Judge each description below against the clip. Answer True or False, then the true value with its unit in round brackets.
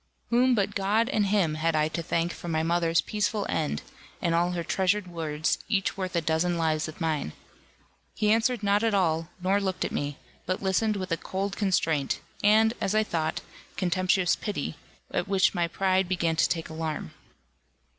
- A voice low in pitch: False (180 Hz)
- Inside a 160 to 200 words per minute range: True (185 wpm)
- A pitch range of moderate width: True (3.7 semitones)